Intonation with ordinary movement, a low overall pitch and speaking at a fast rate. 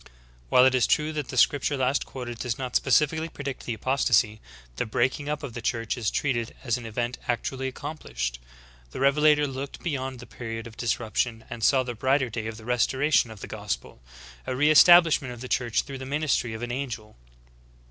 Yes: average, 3.4 semitones; low, 125 Hz; fast, 210 wpm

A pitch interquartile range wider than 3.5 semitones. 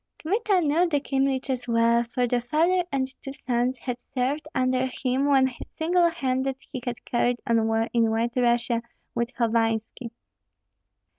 No: average, 2.7 semitones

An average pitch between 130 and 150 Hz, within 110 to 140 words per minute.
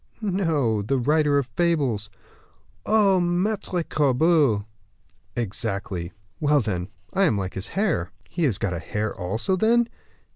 Yes: medium, 140 Hz; slow, 135 wpm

